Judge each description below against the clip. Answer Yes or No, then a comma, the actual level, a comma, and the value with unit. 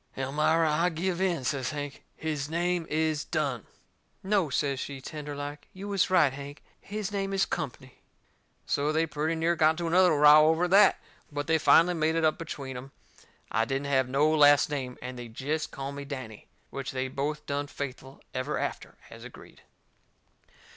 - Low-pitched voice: No, medium, 150 Hz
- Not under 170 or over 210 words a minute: Yes, average, 180 wpm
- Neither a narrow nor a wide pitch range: Yes, average, 3.0 semitones